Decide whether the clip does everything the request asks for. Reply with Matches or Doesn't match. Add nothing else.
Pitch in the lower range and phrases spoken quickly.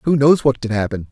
Matches